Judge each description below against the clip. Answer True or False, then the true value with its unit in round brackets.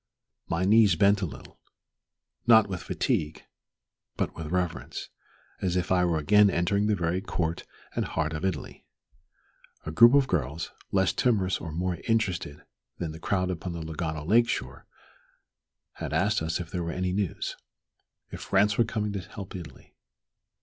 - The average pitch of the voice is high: False (90 Hz)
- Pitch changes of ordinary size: True (3.7 semitones)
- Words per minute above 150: True (160 wpm)